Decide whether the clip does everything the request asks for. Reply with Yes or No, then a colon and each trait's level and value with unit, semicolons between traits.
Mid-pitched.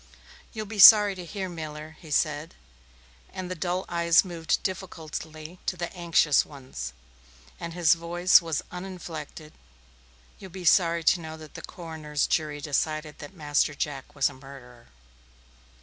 Yes: medium, 165 Hz